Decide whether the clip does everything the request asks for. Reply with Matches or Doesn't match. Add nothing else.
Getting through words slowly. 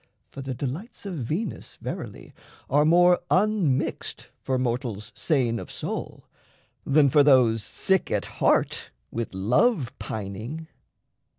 Matches